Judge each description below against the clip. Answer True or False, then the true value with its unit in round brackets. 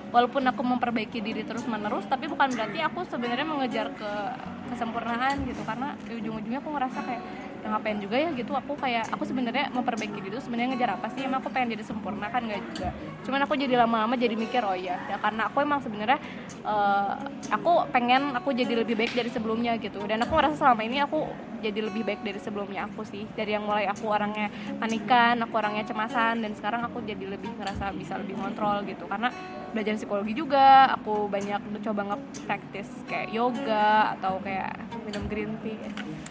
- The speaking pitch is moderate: False (230 Hz)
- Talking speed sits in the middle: False (195 wpm)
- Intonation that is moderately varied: True (3.1 semitones)